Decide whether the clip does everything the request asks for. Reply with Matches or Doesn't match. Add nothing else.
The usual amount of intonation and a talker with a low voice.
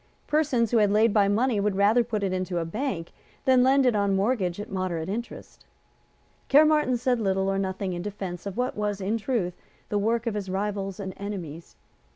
Doesn't match